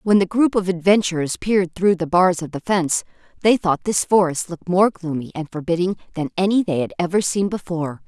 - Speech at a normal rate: No, fast, 210 wpm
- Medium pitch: Yes, medium, 180 Hz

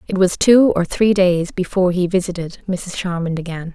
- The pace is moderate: Yes, average, 190 wpm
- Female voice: Yes, female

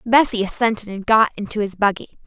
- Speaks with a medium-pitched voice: No, high, 215 Hz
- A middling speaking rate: Yes, average, 185 wpm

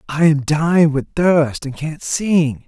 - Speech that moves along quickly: No, average, 180 wpm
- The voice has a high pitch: No, medium, 155 Hz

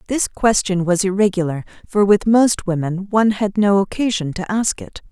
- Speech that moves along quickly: No, average, 175 wpm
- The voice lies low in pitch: No, high, 200 Hz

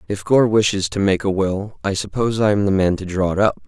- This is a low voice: Yes, low, 100 Hz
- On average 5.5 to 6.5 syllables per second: Yes, 5.9 syllables/s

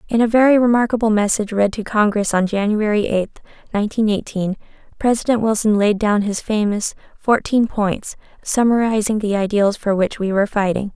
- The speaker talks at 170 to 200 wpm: No, average, 160 wpm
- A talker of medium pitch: No, high, 210 Hz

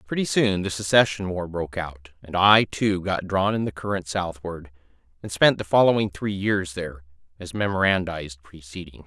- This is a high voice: No, very low, 90 Hz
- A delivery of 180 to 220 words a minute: No, average, 170 wpm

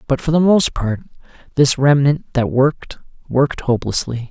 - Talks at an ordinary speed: Yes, average, 155 wpm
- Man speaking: Yes, male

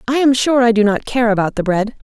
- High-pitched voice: Yes, high, 230 Hz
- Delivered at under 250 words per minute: No, fast, 285 wpm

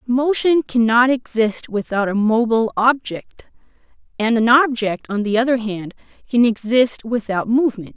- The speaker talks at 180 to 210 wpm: No, slow, 135 wpm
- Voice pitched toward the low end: No, high, 235 Hz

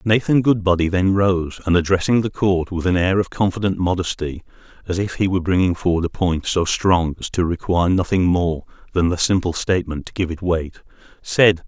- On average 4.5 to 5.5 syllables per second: Yes, 5.4 syllables/s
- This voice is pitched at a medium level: No, very low, 90 Hz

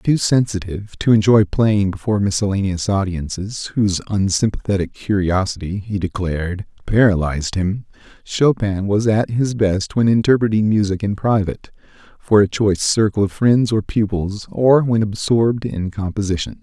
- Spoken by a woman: No, male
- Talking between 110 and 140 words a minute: Yes, slow, 135 wpm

